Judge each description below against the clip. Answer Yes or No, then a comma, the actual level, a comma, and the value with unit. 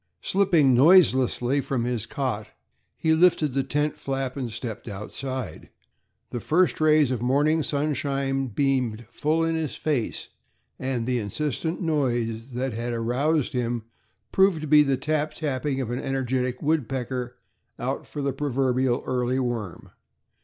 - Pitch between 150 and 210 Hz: No, low, 135 Hz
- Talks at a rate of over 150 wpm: No, average, 140 wpm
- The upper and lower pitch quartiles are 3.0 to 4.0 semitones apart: Yes, average, 3.6 semitones